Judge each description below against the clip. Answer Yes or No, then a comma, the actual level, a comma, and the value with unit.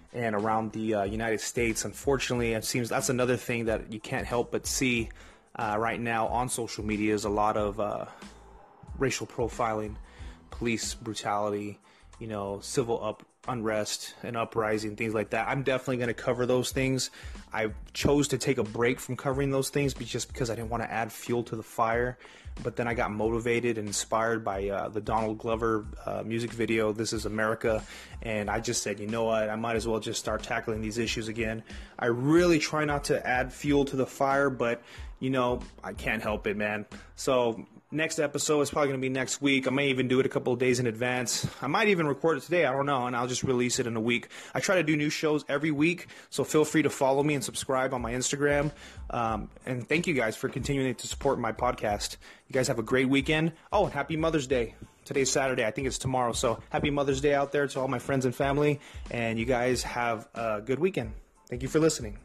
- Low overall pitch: Yes, low, 120 Hz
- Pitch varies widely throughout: No, average, 3.7 semitones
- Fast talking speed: Yes, fast, 225 wpm